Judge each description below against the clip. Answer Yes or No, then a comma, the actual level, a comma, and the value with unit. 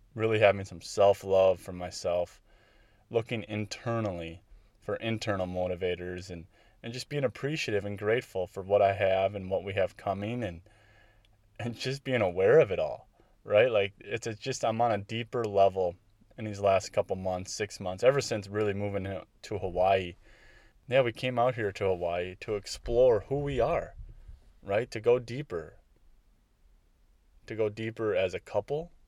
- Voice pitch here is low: Yes, low, 105 Hz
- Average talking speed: Yes, average, 165 wpm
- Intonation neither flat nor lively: Yes, average, 3.4 semitones